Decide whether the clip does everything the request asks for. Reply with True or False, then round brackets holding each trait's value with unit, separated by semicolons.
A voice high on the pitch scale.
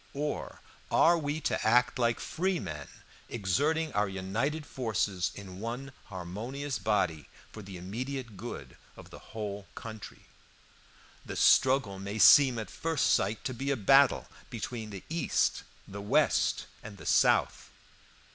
False (110 Hz)